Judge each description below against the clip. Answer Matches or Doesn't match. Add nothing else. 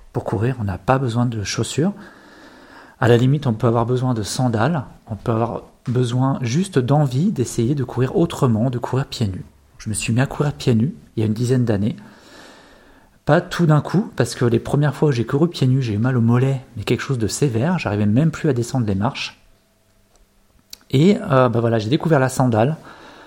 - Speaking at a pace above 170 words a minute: Matches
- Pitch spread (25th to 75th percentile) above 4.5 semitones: Doesn't match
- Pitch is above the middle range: Doesn't match